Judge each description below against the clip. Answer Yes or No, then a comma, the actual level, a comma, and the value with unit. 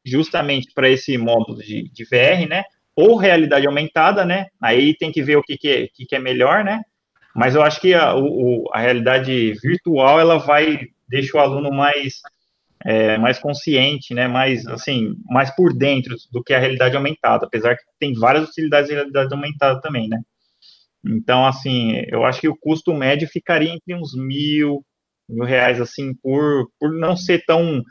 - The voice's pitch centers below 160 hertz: Yes, medium, 140 Hz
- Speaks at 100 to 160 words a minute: No, fast, 185 wpm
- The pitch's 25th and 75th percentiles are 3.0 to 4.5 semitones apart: Yes, average, 3.6 semitones